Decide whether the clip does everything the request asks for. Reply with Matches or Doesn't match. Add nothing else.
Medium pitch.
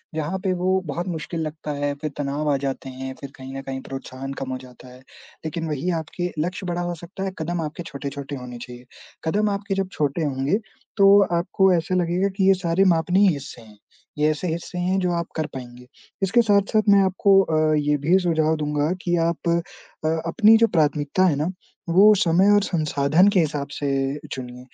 Matches